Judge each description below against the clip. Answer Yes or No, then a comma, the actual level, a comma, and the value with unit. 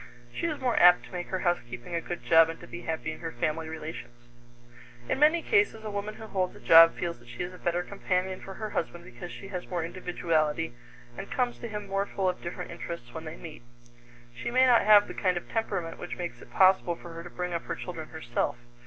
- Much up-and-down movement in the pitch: No, average, 3.4 semitones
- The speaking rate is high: Yes, fast, 240 wpm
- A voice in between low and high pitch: Yes, medium, 175 Hz